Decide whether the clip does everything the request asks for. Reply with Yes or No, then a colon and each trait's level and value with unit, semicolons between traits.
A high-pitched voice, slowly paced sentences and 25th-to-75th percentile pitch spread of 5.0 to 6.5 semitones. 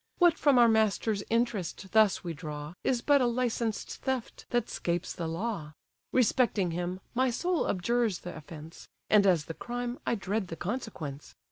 No: high, 215 Hz; average, 165 wpm; wide, 5.6 semitones